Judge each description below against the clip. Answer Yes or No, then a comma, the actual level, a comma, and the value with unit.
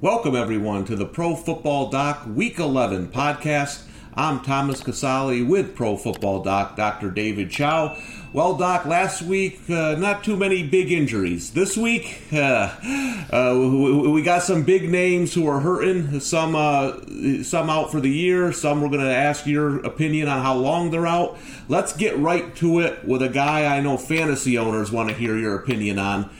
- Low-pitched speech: No, medium, 145 Hz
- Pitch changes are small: No, average, 5.3 semitones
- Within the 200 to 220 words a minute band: No, average, 180 wpm